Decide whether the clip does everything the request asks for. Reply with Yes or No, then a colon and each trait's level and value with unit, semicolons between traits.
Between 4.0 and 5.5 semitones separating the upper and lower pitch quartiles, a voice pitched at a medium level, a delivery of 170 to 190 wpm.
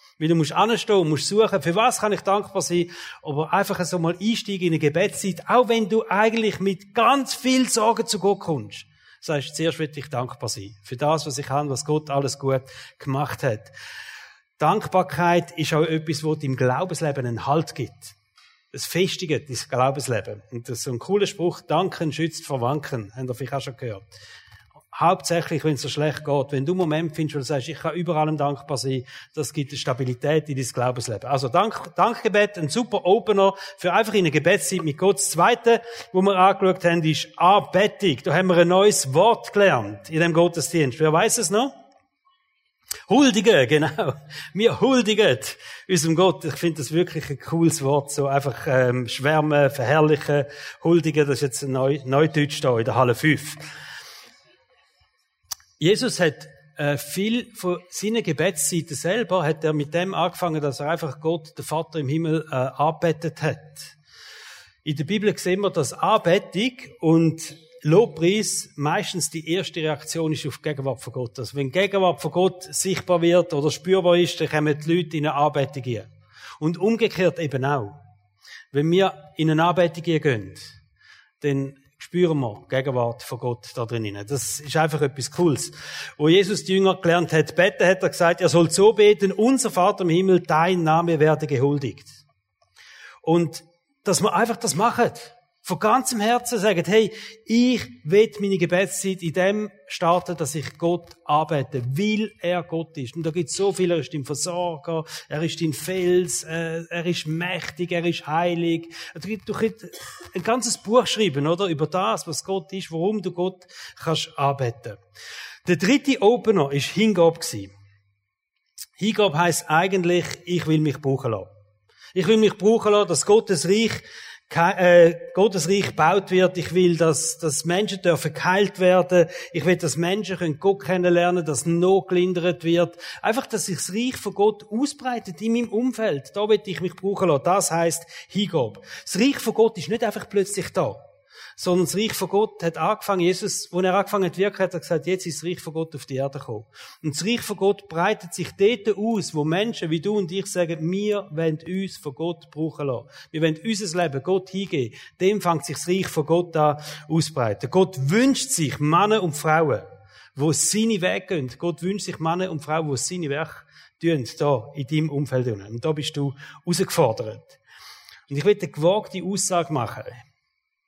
Yes: average, 4.6 semitones; medium, 170 Hz; average, 180 wpm